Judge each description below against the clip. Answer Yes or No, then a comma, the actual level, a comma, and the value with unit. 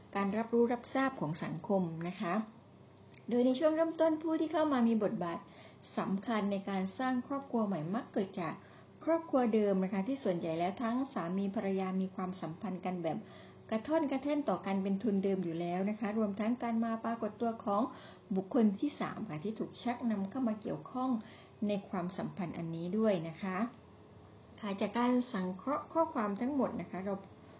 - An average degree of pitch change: Yes, average, 4.4 semitones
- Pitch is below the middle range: No, high, 210 Hz